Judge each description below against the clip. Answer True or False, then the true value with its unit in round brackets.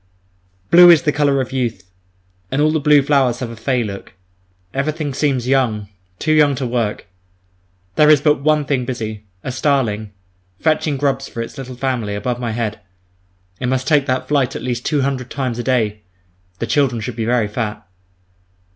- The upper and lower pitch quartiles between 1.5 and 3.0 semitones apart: False (3.9 semitones)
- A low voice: True (130 Hz)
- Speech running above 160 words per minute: True (180 wpm)